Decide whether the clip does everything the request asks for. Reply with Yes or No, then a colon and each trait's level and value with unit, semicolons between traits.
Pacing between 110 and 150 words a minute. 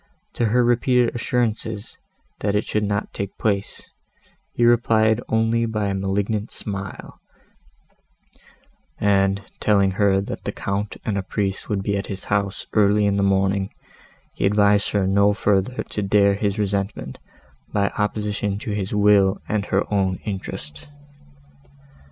Yes: average, 145 wpm